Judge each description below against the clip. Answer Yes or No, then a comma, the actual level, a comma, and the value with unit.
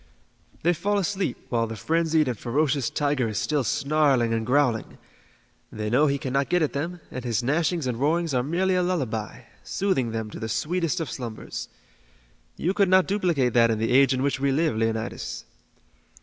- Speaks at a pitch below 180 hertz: Yes, medium, 140 Hz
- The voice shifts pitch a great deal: Yes, wide, 6.0 semitones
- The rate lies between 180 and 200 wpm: Yes, average, 185 wpm